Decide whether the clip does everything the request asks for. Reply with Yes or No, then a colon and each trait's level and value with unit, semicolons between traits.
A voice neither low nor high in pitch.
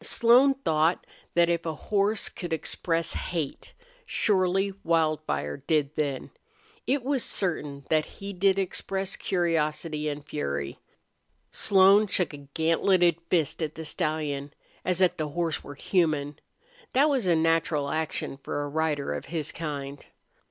Yes: medium, 160 Hz